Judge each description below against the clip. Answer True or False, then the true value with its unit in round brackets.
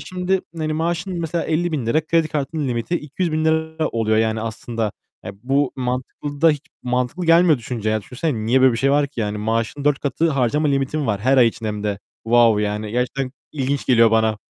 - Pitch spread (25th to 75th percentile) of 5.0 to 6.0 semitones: True (5.4 semitones)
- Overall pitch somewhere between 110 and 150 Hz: True (135 Hz)